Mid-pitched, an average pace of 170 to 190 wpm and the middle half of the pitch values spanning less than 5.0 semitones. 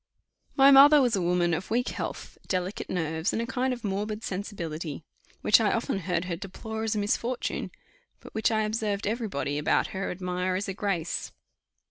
No: high, 200 Hz; average, 185 wpm; average, 3.8 semitones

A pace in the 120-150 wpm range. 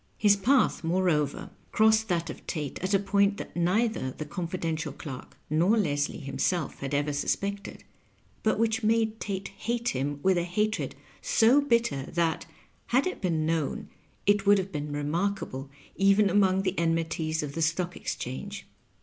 No: average, 160 wpm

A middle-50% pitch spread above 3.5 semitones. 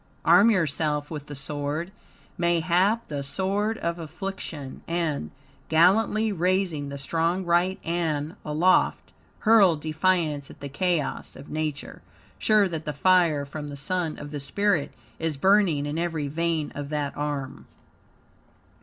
Yes: average, 4.0 semitones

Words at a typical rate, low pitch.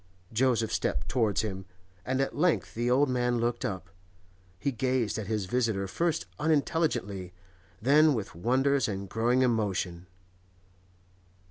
No: slow, 130 wpm; low, 120 Hz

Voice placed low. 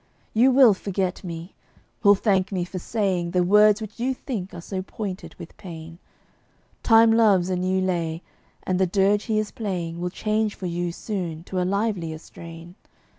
No: high, 190 Hz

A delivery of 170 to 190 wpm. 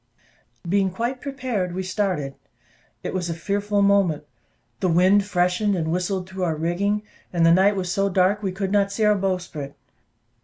Yes: average, 180 wpm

